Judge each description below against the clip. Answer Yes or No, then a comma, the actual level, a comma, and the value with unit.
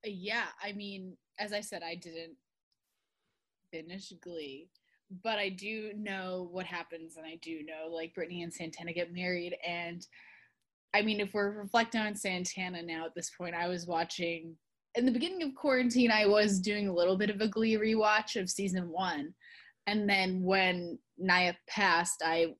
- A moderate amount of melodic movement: Yes, average, 3.6 semitones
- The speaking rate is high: No, average, 175 wpm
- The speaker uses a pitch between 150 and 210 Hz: Yes, medium, 185 Hz